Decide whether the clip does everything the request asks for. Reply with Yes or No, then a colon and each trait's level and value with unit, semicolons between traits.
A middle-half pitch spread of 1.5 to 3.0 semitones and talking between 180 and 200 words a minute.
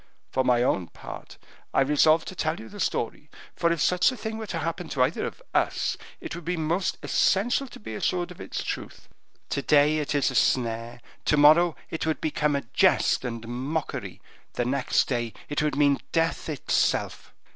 No: average, 4.7 semitones; average, 195 wpm